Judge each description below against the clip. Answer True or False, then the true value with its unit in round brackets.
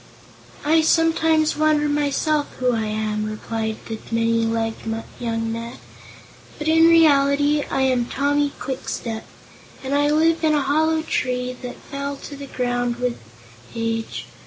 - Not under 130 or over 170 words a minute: True (140 wpm)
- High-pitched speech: True (270 Hz)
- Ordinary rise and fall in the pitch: True (4.6 semitones)